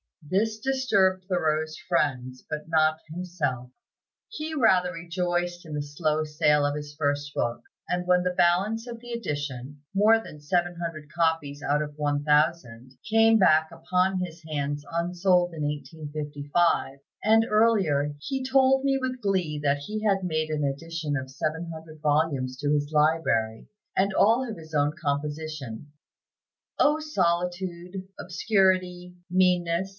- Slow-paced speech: No, average, 145 wpm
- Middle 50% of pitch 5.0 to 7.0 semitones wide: No, average, 4.2 semitones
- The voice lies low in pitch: No, medium, 165 Hz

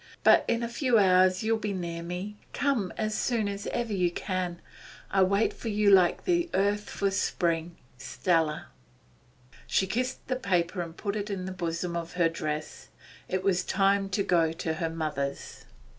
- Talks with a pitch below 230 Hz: Yes, medium, 185 Hz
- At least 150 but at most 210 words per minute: Yes, average, 185 wpm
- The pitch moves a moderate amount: Yes, average, 3.5 semitones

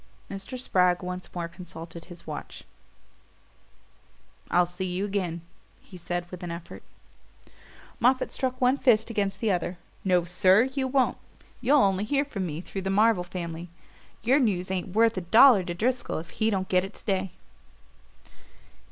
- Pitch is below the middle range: No, high, 190 Hz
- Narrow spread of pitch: No, average, 4.3 semitones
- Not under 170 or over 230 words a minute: No, average, 160 wpm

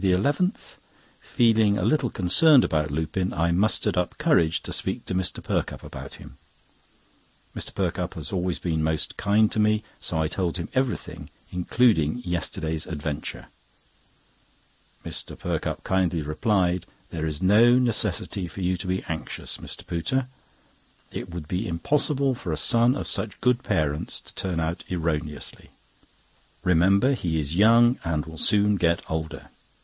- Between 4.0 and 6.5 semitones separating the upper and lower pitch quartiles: Yes, average, 5.1 semitones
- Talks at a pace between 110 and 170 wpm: Yes, average, 145 wpm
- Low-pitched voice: Yes, very low, 90 Hz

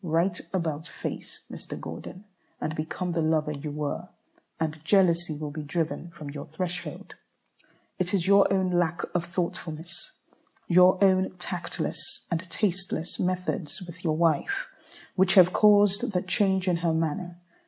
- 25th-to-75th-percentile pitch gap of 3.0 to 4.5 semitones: No, narrow, 2.6 semitones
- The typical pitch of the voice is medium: Yes, medium, 175 Hz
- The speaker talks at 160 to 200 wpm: No, average, 145 wpm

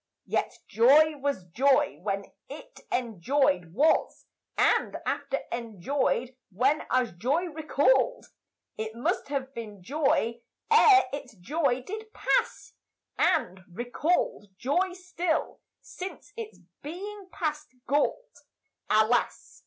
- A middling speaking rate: No, slow, 105 wpm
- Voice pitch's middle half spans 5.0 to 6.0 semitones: Yes, wide, 5.5 semitones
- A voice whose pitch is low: No, very high, 275 Hz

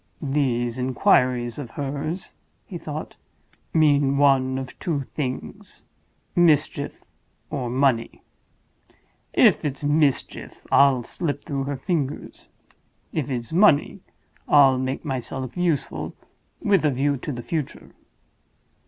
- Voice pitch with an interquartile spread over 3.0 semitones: No, narrow, 2.5 semitones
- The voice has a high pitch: No, medium, 140 Hz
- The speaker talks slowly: Yes, slow, 110 wpm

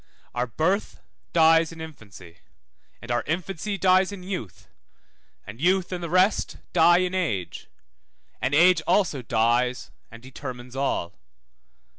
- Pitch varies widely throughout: Yes, wide, 7.0 semitones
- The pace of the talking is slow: Yes, slow, 130 wpm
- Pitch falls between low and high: Yes, medium, 160 Hz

